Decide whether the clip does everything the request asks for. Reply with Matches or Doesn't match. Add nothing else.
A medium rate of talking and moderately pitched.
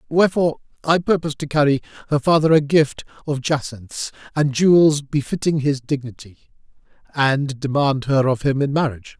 Matches